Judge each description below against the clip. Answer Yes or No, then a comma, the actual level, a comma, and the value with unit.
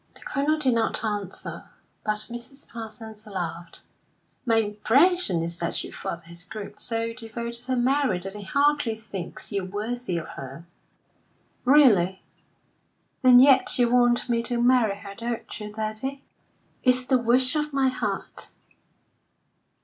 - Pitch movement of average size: Yes, average, 3.8 semitones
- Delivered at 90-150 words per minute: Yes, average, 140 wpm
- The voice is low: No, high, 230 Hz